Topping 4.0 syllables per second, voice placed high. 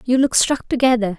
Yes: 5.5 syllables/s; high, 240 Hz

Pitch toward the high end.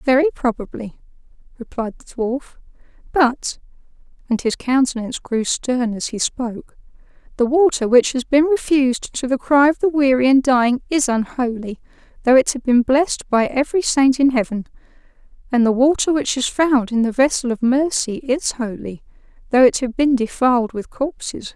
Yes: very high, 255 Hz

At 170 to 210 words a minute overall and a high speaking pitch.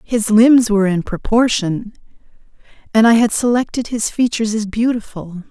No: average, 140 wpm; high, 220 Hz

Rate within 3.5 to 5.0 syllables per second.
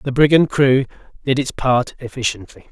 Yes: 4.9 syllables/s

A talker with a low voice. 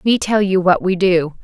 No: medium, 185 Hz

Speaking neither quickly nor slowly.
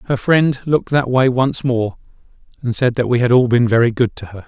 No: fast, 240 wpm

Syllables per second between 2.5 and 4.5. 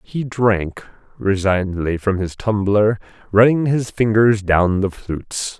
Yes: 4.0 syllables/s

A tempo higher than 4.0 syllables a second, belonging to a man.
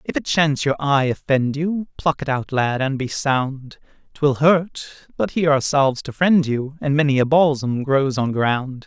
Yes: 4.7 syllables/s; male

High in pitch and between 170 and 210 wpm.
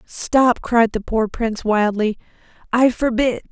No: high, 230 Hz; slow, 135 wpm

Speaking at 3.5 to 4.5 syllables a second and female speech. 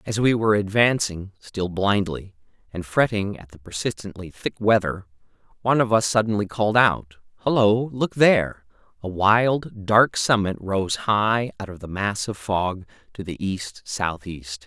No: 4.4 syllables/s; male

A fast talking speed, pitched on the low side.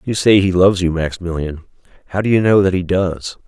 Yes: fast, 225 wpm; very low, 90 Hz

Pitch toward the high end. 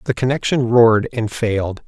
No: low, 115 Hz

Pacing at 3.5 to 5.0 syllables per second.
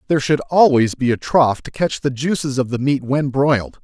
No: 5.3 syllables/s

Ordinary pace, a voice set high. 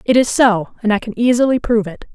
No: fast, 250 wpm; high, 225 Hz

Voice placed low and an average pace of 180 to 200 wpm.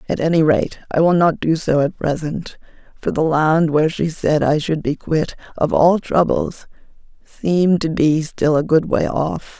No: medium, 160 Hz; average, 195 wpm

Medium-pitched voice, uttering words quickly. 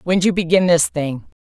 Yes: medium, 170 Hz; fast, 210 wpm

